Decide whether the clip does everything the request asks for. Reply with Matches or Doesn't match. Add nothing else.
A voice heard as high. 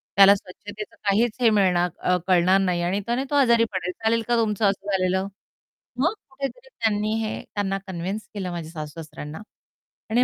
Matches